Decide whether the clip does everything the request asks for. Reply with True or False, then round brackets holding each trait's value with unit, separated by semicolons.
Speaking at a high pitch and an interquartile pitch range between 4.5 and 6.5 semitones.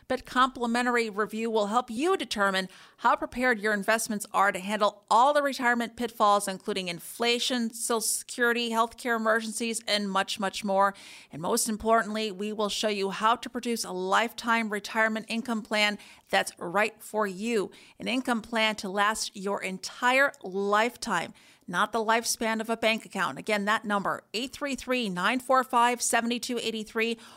False (225 Hz; 2.4 semitones)